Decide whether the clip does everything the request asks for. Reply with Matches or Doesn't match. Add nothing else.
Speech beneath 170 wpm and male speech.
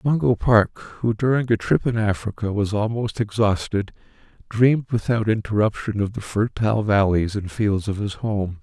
Matches